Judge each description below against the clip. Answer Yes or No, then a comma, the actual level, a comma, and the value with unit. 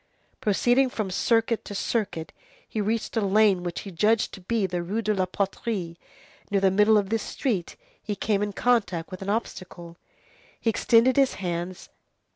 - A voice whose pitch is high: Yes, high, 205 Hz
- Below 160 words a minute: No, average, 175 wpm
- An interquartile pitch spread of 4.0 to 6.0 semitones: No, average, 3.4 semitones